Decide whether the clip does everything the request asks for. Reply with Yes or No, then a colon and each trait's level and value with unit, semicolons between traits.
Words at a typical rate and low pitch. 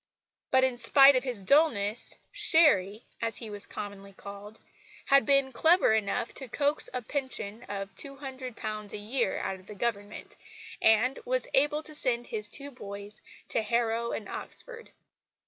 No: average, 155 wpm; high, 235 Hz